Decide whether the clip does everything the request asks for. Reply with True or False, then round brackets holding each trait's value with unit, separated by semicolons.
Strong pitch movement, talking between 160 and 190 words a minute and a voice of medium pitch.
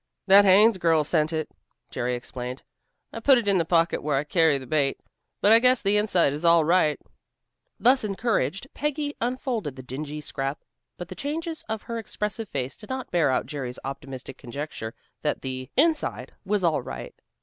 True (8.0 semitones; 185 wpm; 170 Hz)